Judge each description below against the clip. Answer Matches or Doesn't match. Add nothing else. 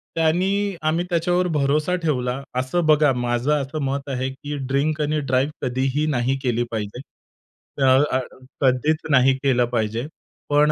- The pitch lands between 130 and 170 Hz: Matches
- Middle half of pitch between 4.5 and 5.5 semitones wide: Doesn't match